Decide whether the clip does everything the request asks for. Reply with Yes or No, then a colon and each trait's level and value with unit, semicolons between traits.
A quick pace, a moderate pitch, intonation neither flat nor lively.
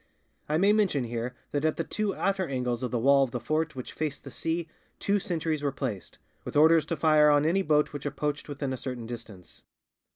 Yes: fast, 220 wpm; medium, 145 Hz; average, 4.1 semitones